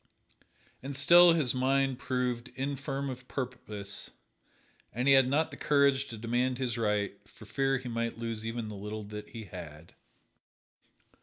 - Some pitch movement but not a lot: Yes, average, 3.5 semitones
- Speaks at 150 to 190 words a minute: Yes, average, 155 wpm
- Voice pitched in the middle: No, low, 125 Hz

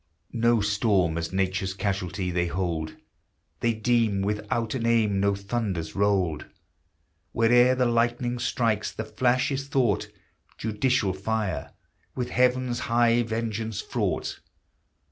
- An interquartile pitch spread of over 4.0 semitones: No, average, 3.7 semitones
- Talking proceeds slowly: Yes, slow, 120 wpm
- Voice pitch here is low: Yes, low, 110 Hz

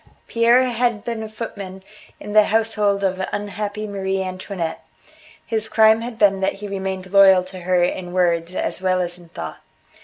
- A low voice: No, high, 195 Hz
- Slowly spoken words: No, average, 175 wpm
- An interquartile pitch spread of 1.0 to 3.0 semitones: Yes, average, 2.7 semitones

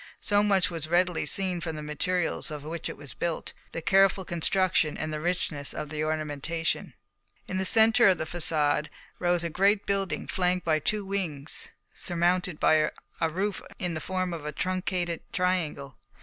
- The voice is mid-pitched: Yes, medium, 175 Hz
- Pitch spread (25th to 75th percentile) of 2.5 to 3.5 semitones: Yes, average, 3.2 semitones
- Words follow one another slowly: No, average, 175 wpm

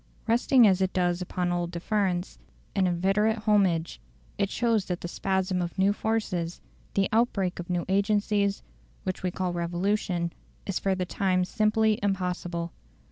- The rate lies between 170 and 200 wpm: No, average, 150 wpm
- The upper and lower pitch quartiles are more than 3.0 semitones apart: No, average, 2.7 semitones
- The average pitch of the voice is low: No, high, 190 Hz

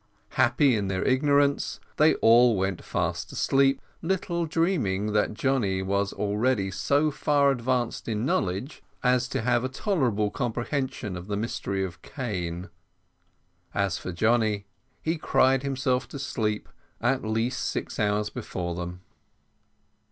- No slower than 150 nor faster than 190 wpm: No, slow, 135 wpm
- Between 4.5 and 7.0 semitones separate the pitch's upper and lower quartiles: Yes, average, 5.1 semitones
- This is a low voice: Yes, low, 120 Hz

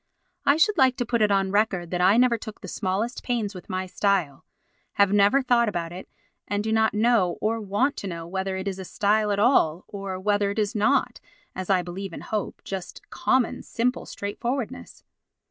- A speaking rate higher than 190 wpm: Yes, average, 200 wpm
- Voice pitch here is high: Yes, high, 205 Hz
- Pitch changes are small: No, average, 3.3 semitones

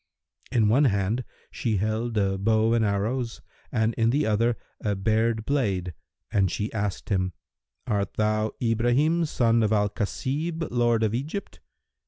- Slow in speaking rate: No, average, 150 wpm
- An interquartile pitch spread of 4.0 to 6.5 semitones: No, average, 2.7 semitones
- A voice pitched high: No, low, 110 Hz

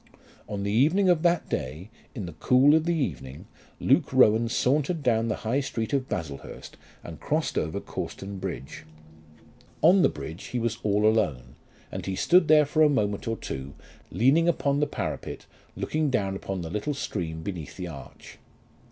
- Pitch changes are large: Yes, wide, 8.2 semitones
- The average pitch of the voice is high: No, low, 110 Hz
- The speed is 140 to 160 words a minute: No, average, 175 wpm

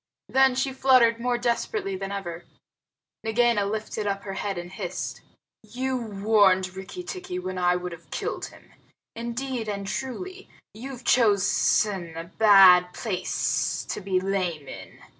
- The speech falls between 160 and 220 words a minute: No, average, 140 wpm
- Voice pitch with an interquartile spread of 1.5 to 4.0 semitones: No, average, 4.6 semitones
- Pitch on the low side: No, high, 205 Hz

